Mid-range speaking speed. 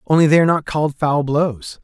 No: fast, 230 wpm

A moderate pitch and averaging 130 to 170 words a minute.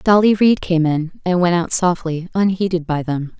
No: medium, 175 Hz; average, 195 wpm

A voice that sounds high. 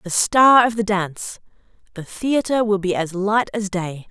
Yes: high, 205 Hz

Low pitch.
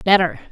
No: medium, 175 Hz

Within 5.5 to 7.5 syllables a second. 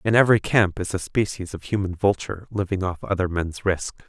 Yes: 5.6 syllables/s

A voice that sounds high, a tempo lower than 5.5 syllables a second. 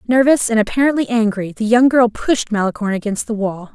No: high, 225 Hz; 6.0 syllables/s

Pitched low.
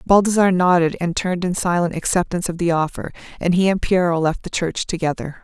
No: medium, 175 Hz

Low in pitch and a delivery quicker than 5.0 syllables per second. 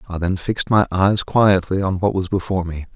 Yes: very low, 95 Hz; 5.6 syllables/s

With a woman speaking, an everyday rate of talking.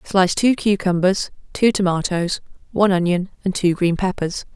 Yes: female; average, 145 wpm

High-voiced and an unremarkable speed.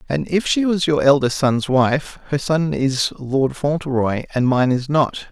No: medium, 140 Hz; average, 190 wpm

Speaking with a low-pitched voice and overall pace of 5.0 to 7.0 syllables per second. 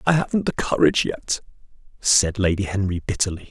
Yes: low, 105 Hz; 5.8 syllables/s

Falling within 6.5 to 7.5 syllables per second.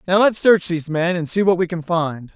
No: 5.5 syllables/s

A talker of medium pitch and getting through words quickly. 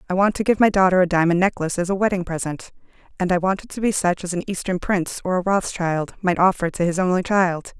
Yes: medium, 180 Hz; fast, 255 wpm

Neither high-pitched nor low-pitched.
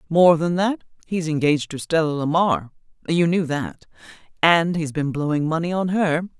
Yes: medium, 160 Hz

